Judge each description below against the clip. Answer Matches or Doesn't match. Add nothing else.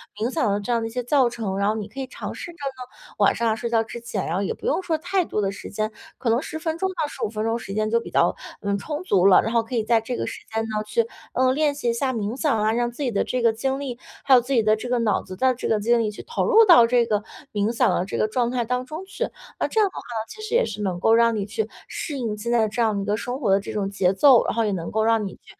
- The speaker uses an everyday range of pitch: Matches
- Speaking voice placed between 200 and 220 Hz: Doesn't match